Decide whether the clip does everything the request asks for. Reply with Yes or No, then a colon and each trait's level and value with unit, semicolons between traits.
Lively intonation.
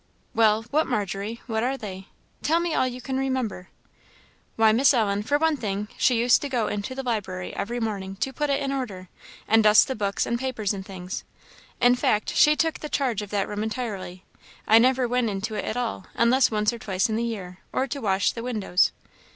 No: average, 4.1 semitones